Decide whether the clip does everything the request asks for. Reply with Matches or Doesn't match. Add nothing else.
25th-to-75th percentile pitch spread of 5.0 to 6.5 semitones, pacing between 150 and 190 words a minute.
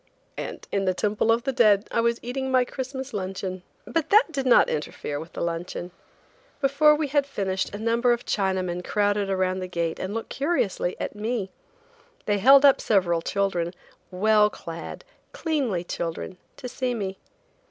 Matches